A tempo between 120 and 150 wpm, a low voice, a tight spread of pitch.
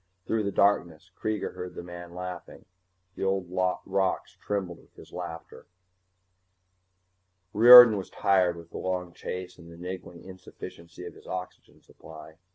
Yes: average, 145 wpm; very low, 90 Hz; narrow, 2.0 semitones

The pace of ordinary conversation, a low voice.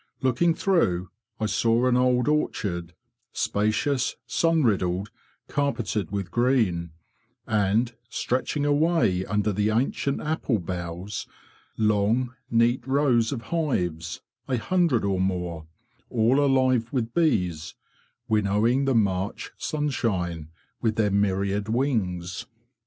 No: slow, 110 wpm; low, 110 Hz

